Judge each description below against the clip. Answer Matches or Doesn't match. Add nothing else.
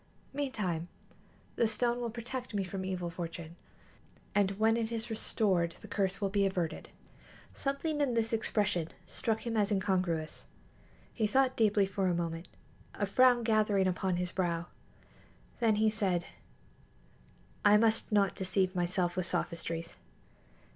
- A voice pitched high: Matches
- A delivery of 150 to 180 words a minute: Doesn't match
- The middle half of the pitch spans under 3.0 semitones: Doesn't match